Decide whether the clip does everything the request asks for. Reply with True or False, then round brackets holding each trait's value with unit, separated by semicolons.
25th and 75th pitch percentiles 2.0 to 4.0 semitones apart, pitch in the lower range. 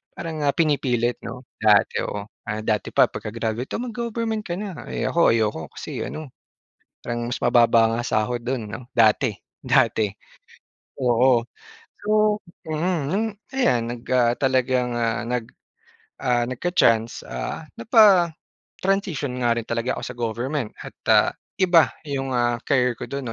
False (5.1 semitones; 125 Hz)